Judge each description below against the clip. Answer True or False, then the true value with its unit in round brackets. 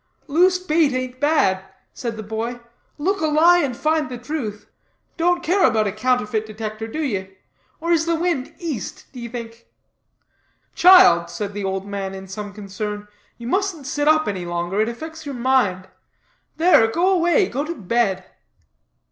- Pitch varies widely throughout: True (7.3 semitones)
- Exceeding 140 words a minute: True (165 wpm)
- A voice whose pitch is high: True (245 Hz)